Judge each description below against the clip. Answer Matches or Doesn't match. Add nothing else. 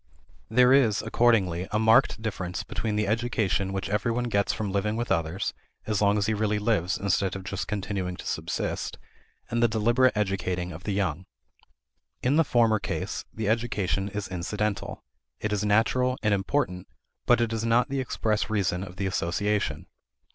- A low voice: Matches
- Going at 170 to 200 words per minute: Matches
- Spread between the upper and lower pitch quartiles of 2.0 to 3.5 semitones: Matches